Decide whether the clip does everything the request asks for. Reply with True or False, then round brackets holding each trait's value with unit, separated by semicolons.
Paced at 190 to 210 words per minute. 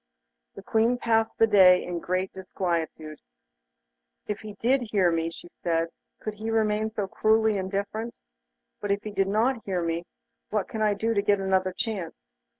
False (170 wpm)